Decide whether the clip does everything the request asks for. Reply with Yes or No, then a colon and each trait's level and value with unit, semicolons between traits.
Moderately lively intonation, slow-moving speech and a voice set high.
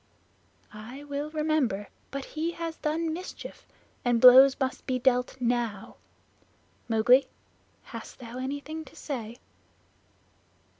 Yes: average, 4.0 semitones; slow, 110 wpm; very high, 265 Hz